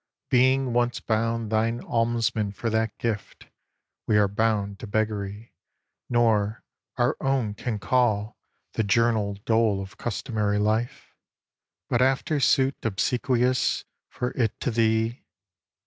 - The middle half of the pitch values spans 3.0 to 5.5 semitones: No, narrow, 2.5 semitones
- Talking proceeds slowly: Yes, slow, 120 wpm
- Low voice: Yes, low, 115 Hz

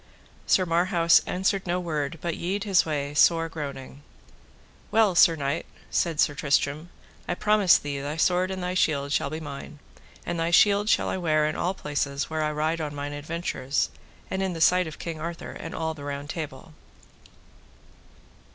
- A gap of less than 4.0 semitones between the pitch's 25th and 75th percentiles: Yes, average, 3.4 semitones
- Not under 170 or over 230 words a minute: Yes, average, 180 wpm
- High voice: No, medium, 160 Hz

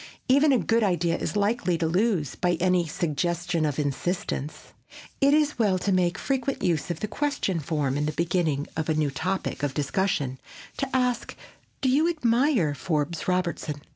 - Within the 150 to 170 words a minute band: Yes, average, 165 wpm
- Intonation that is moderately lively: No, wide, 6.8 semitones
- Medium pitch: Yes, medium, 180 Hz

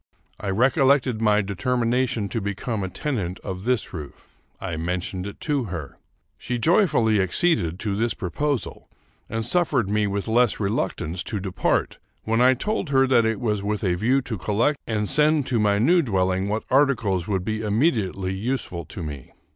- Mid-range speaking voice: No, low, 110 Hz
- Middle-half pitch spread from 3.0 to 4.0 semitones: No, average, 4.8 semitones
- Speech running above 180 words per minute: No, average, 175 wpm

